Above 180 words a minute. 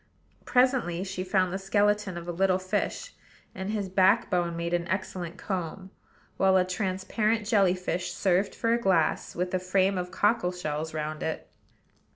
No: average, 165 wpm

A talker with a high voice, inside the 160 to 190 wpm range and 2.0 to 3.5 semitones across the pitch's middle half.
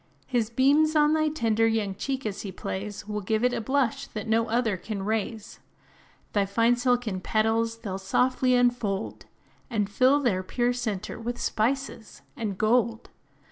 Yes: high, 225 Hz; average, 165 wpm; average, 2.9 semitones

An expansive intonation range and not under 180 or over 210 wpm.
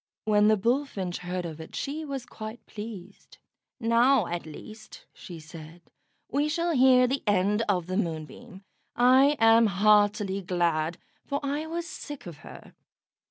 No: wide, 6.5 semitones; average, 150 wpm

